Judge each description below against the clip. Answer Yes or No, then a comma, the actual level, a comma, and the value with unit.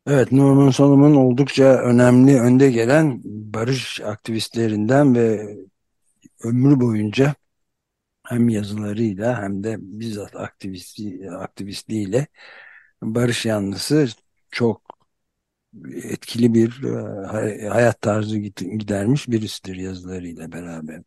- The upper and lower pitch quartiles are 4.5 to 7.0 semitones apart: No, average, 3.8 semitones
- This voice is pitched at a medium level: No, low, 110 Hz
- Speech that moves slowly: Yes, slow, 85 wpm